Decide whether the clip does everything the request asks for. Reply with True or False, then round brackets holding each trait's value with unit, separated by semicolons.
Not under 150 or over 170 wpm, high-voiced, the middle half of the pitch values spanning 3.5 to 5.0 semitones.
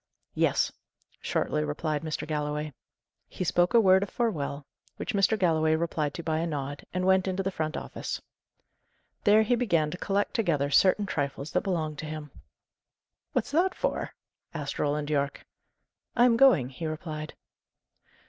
False (160 wpm; 160 Hz; 4.4 semitones)